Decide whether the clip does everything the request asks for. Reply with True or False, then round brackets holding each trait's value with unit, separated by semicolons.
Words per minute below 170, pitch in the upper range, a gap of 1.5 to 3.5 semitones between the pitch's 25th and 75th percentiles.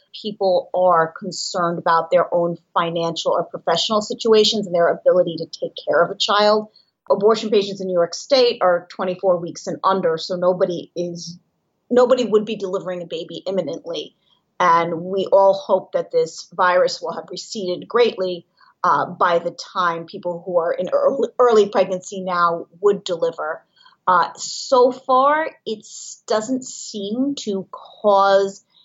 False (150 wpm; 195 Hz; 4.0 semitones)